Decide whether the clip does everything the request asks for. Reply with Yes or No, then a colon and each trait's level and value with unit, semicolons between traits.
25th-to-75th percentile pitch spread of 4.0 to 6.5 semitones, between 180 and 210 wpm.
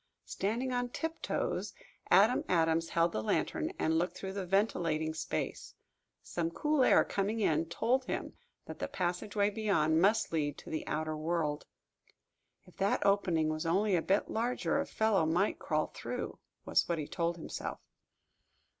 No: average, 4.5 semitones; average, 160 wpm